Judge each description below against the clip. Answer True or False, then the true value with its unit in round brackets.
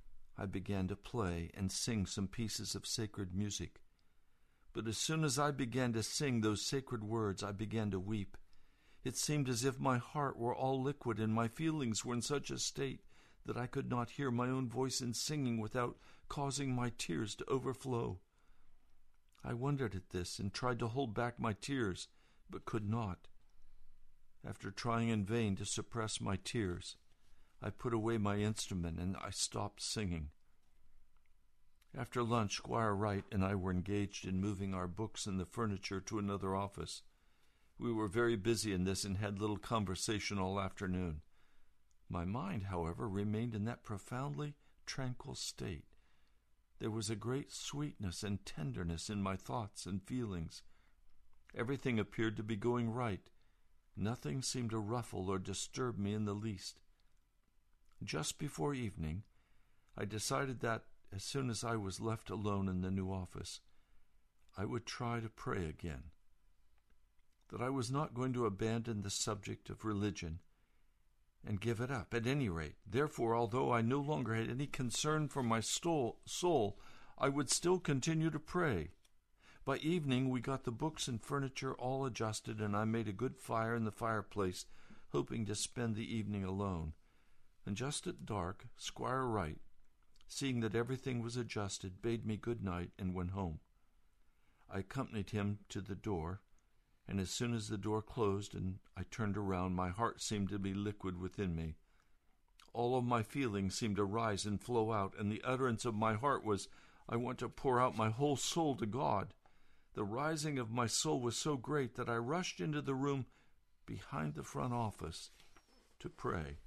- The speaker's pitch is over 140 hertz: False (110 Hz)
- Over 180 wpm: False (170 wpm)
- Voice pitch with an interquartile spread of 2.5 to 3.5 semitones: False (4.5 semitones)